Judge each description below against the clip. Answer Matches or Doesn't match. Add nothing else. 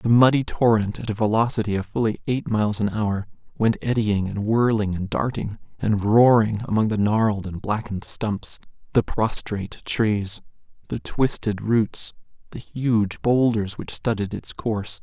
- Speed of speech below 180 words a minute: Matches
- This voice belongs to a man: Matches